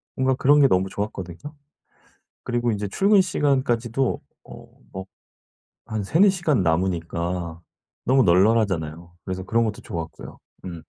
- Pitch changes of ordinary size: No, wide, 6.8 semitones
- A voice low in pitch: Yes, low, 105 Hz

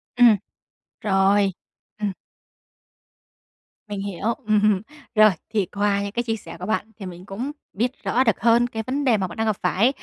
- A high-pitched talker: Yes, high, 210 Hz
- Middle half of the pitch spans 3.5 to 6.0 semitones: No, average, 2.8 semitones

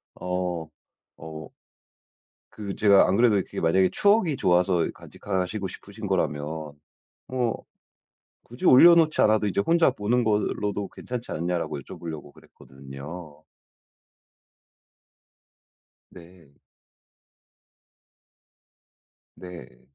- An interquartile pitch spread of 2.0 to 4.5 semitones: No, average, 5.2 semitones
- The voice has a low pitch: Yes, very low, 90 Hz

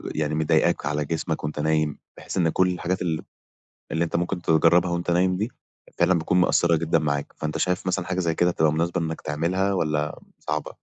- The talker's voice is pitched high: No, very low, 85 Hz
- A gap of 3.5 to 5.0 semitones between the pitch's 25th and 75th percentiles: No, narrow, 2.5 semitones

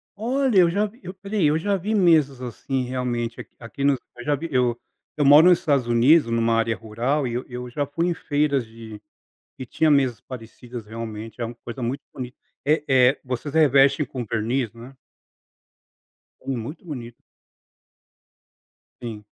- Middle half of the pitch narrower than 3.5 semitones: No, average, 4.3 semitones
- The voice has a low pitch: Yes, low, 130 Hz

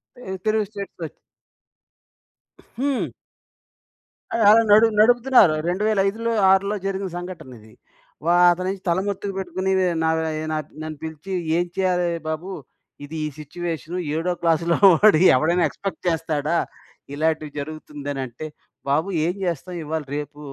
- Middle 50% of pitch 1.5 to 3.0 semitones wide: No, average, 3.9 semitones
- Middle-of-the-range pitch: Yes, medium, 175 Hz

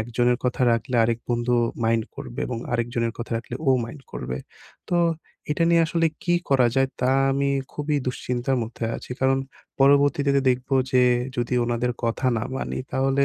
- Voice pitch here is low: Yes, low, 125 Hz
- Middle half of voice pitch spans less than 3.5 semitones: Yes, narrow, 2.6 semitones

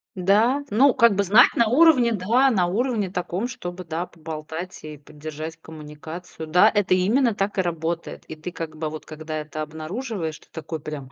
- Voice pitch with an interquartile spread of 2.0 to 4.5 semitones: No, average, 5.3 semitones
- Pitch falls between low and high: Yes, medium, 175 Hz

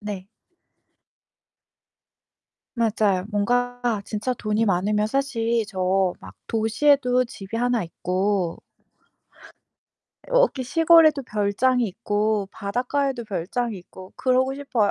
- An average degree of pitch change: Yes, average, 3.9 semitones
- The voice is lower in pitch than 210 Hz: No, high, 220 Hz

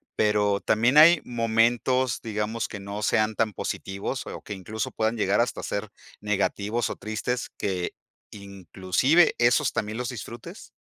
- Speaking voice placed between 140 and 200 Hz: No, low, 110 Hz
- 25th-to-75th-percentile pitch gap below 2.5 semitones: No, average, 2.8 semitones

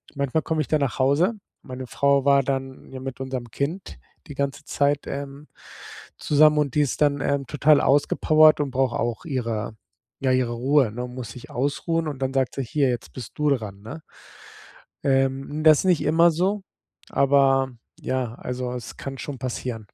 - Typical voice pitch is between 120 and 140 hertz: Yes, low, 135 Hz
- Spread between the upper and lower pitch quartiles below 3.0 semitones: Yes, narrow, 2.4 semitones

